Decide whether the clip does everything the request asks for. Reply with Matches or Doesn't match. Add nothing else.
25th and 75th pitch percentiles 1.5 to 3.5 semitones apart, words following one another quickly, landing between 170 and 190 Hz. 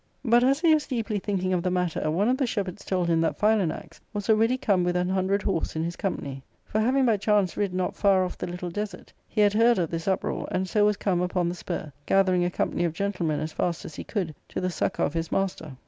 Matches